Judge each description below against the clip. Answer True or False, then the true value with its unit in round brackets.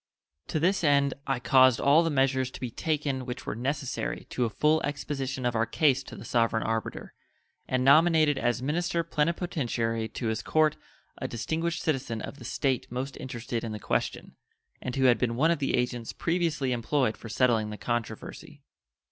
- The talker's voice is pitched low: True (130 Hz)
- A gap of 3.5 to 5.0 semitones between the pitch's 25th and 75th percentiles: True (4.1 semitones)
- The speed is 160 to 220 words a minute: True (180 wpm)